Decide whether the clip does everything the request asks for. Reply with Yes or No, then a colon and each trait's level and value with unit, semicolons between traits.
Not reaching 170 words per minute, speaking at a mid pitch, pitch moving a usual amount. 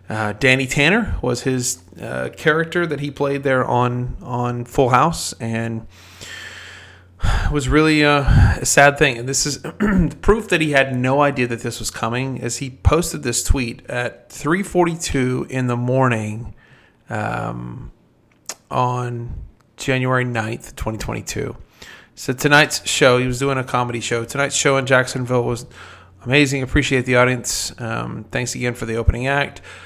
No: average, 150 wpm; low, 125 Hz; average, 3.6 semitones